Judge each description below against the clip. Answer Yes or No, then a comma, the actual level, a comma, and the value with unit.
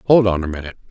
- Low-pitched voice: Yes, very low, 95 Hz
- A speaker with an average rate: No, fast, 265 wpm